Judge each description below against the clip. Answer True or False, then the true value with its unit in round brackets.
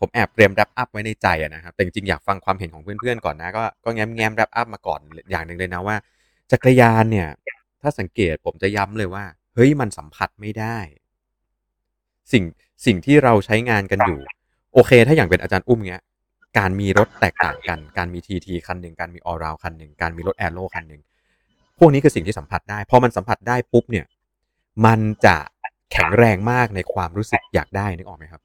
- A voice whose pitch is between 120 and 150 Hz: False (100 Hz)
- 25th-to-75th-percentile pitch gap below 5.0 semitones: True (4.5 semitones)